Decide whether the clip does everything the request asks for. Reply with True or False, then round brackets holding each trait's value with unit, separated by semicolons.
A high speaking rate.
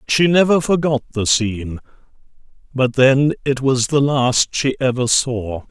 False (145 wpm)